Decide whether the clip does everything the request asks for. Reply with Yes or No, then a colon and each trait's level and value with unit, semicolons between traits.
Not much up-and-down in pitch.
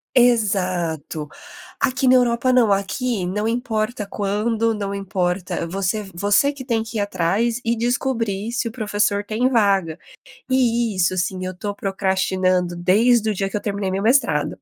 No: average, 3.7 semitones